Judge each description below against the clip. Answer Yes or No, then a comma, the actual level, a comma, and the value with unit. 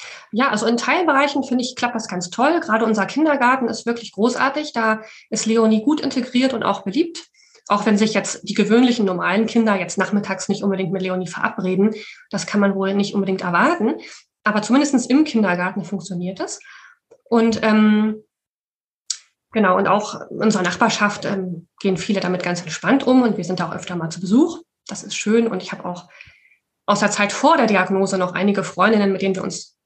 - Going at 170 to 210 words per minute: Yes, fast, 190 wpm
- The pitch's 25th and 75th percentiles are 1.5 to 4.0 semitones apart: No, average, 4.4 semitones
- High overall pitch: Yes, high, 215 Hz